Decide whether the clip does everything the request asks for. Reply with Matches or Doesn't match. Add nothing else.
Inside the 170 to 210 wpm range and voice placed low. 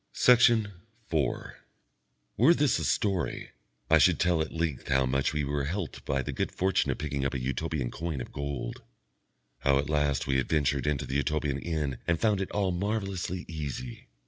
Matches